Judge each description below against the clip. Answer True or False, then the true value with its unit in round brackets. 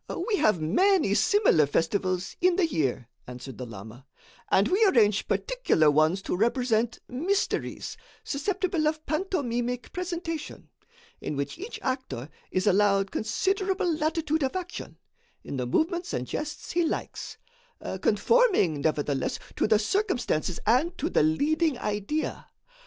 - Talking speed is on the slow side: True (130 wpm)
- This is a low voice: False (250 Hz)